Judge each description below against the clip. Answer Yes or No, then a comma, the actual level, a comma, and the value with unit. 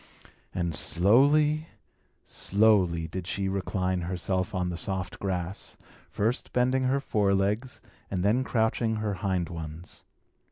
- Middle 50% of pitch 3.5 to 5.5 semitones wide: Yes, average, 3.8 semitones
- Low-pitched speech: Yes, low, 100 Hz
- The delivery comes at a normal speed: No, slow, 125 wpm